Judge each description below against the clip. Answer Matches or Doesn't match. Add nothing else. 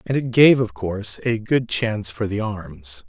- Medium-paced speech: Doesn't match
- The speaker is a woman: Doesn't match